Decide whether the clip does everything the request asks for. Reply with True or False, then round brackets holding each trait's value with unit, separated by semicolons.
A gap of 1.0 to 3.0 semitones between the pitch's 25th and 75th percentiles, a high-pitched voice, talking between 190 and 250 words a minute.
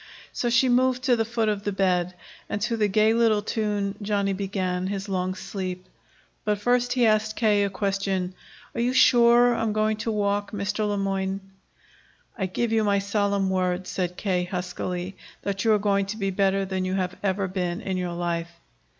True (2.5 semitones; 200 Hz; 195 wpm)